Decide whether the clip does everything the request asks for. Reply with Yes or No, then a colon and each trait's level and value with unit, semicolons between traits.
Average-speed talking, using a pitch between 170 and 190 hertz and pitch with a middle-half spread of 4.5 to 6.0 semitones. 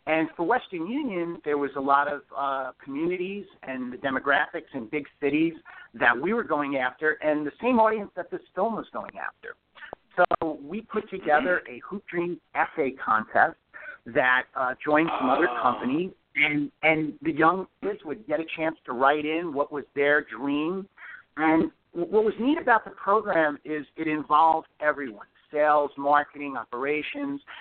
No: average, 165 wpm; medium, 155 Hz; average, 4.8 semitones